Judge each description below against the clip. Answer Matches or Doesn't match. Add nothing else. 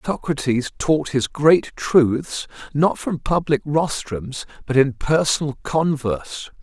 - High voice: Doesn't match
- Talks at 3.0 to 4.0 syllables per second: Matches